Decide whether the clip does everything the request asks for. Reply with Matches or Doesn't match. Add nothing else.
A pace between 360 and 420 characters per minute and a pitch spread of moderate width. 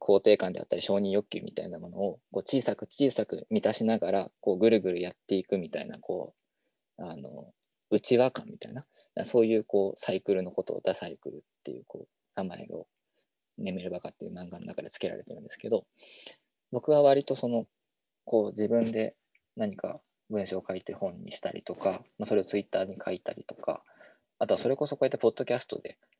Matches